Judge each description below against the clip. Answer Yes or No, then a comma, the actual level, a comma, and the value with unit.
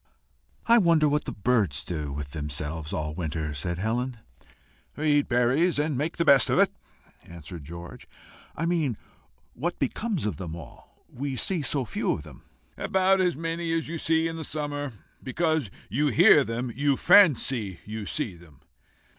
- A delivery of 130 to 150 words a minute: No, average, 165 wpm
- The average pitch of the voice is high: No, low, 130 Hz